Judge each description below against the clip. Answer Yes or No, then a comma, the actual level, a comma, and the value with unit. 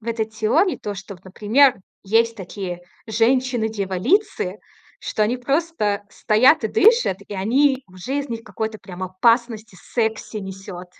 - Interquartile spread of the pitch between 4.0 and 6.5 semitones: Yes, average, 4.4 semitones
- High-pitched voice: Yes, high, 220 Hz